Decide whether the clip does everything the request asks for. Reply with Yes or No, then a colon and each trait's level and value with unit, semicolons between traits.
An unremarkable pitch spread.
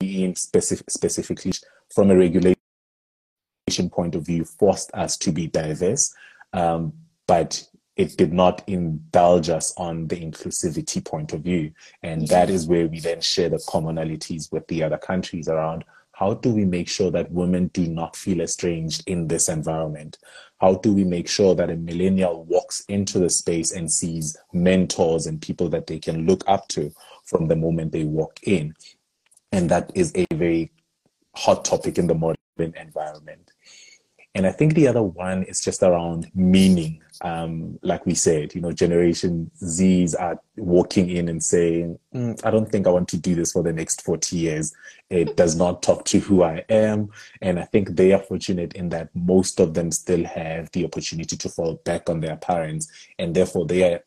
No: narrow, 2.3 semitones